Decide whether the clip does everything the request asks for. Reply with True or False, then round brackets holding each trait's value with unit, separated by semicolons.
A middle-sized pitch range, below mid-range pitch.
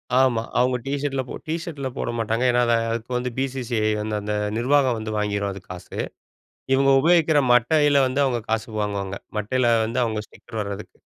True (3.7 semitones; 120 Hz)